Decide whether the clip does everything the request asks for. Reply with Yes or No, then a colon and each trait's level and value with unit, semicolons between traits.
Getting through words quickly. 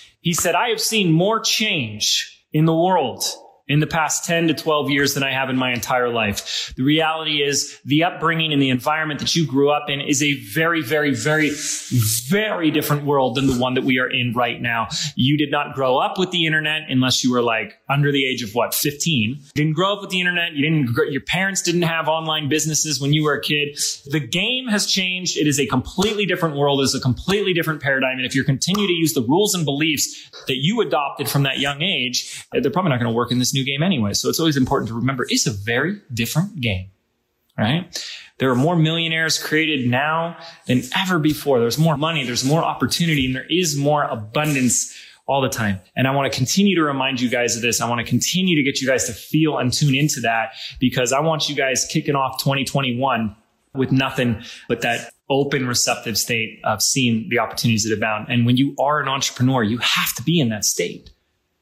Yes: fast, 220 wpm